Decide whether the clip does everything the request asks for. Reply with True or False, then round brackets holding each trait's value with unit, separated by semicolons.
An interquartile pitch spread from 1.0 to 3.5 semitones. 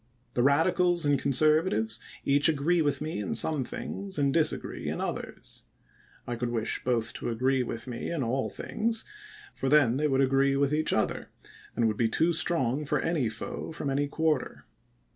False (4.3 semitones)